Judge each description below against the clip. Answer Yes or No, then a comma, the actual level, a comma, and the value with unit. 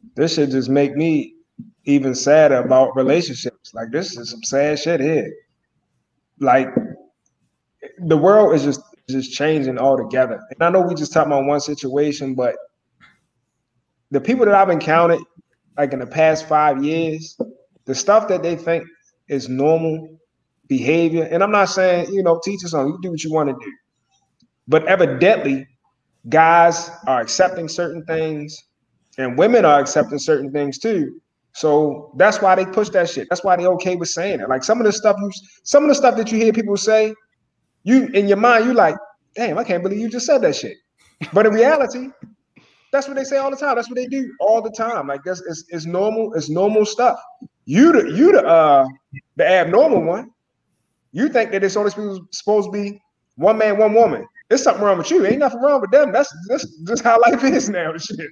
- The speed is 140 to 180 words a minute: No, average, 195 wpm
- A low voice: No, medium, 175 Hz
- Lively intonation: Yes, wide, 6.9 semitones